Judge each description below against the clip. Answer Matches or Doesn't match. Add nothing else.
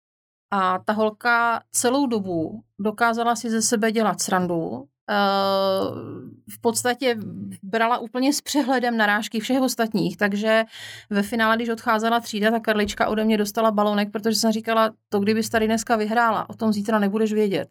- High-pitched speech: Matches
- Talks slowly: Doesn't match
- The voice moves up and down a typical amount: Doesn't match